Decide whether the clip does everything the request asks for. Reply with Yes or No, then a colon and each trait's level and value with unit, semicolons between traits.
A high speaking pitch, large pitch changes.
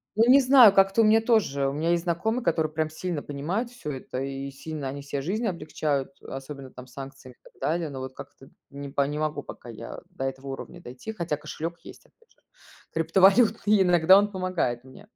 No: medium, 155 Hz; wide, 6.0 semitones